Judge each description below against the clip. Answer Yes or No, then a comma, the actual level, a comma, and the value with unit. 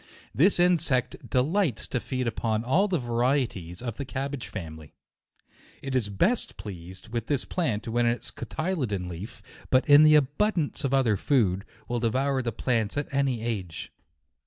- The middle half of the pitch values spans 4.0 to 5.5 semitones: Yes, average, 4.7 semitones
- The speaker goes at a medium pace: Yes, average, 165 wpm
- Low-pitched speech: Yes, low, 125 Hz